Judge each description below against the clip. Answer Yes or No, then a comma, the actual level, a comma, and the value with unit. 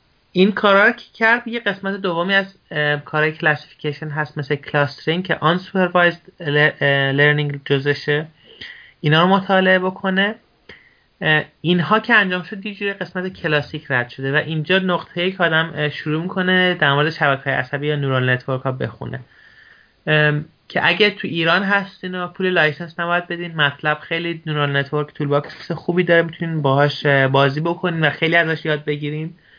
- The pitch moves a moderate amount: Yes, average, 3.7 semitones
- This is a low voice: No, medium, 160 Hz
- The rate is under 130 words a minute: No, average, 150 wpm